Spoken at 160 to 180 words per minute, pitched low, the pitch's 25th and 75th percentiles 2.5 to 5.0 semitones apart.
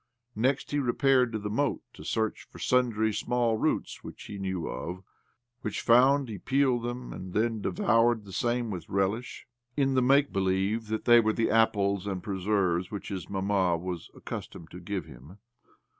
Yes: average, 175 wpm; low, 110 Hz; average, 4.0 semitones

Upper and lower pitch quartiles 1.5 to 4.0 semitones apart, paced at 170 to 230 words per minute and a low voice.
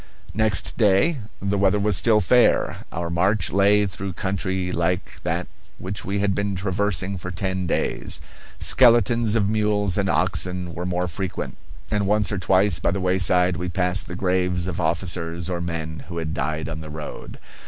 Yes: narrow, 2.6 semitones; average, 175 wpm; very low, 95 Hz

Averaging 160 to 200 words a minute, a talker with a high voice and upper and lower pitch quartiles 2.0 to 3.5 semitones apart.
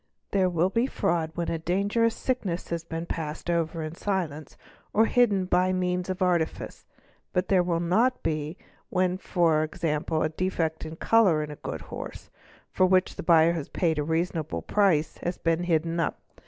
No: average, 180 wpm; medium, 170 Hz; narrow, 2.5 semitones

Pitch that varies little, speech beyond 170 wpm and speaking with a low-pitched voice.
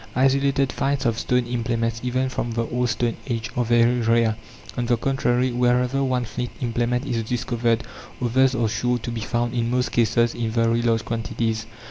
Yes: narrow, 1.4 semitones; average, 180 wpm; low, 120 Hz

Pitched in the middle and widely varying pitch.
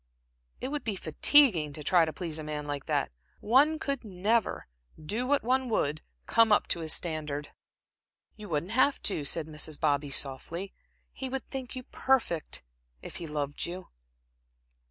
Yes: medium, 175 Hz; wide, 8.5 semitones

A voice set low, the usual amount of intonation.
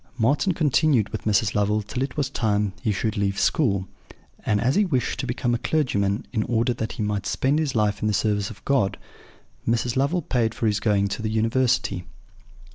Yes: low, 110 Hz; average, 4.0 semitones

